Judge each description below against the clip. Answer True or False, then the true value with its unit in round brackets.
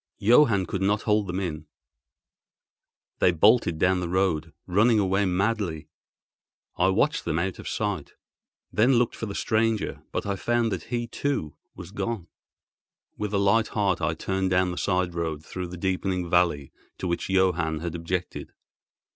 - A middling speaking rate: True (165 wpm)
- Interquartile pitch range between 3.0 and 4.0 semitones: True (3.4 semitones)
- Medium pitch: False (95 Hz)